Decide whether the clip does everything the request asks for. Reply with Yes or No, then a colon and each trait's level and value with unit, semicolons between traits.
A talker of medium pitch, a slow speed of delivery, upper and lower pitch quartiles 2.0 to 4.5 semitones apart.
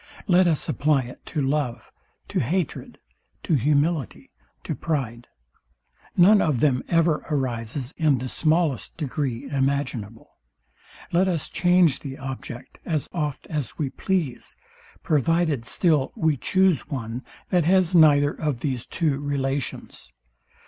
Yes: medium, 145 Hz; slow, 130 wpm; average, 3.8 semitones